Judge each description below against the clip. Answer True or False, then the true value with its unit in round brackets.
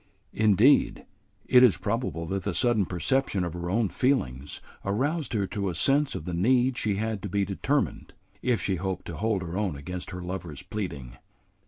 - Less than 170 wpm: False (185 wpm)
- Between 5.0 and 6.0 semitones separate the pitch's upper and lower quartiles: True (5.3 semitones)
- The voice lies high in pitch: False (100 Hz)